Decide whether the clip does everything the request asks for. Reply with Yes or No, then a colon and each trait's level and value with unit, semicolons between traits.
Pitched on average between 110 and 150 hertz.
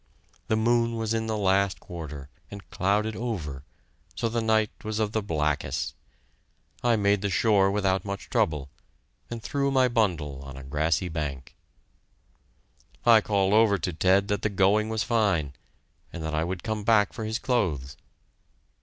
No: low, 100 Hz